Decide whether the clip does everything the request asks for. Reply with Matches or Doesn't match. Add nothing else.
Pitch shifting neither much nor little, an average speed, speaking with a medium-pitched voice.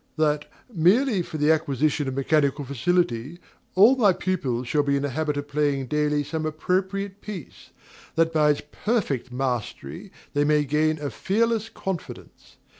Matches